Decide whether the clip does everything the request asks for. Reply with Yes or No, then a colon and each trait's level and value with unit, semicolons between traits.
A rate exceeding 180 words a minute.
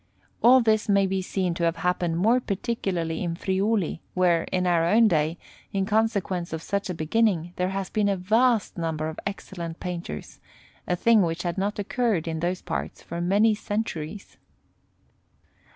No: average, 170 wpm